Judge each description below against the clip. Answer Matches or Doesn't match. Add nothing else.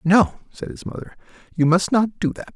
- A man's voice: Matches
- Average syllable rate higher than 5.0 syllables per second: Matches